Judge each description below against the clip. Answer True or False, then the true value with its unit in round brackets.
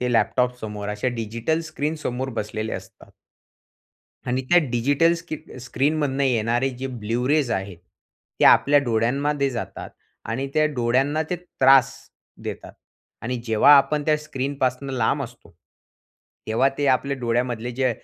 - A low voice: True (130 Hz)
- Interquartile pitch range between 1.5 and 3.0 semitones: False (3.4 semitones)